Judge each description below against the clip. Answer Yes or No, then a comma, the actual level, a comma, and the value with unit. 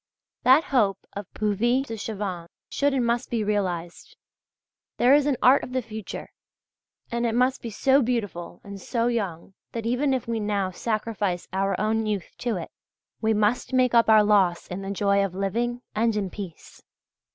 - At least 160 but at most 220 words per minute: Yes, average, 180 wpm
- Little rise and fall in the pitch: No, average, 3.4 semitones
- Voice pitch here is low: No, high, 220 Hz